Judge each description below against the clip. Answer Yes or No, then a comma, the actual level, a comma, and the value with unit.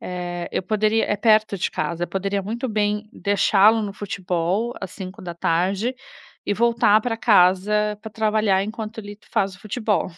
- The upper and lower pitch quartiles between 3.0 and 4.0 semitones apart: No, narrow, 2.4 semitones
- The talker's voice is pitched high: Yes, high, 205 Hz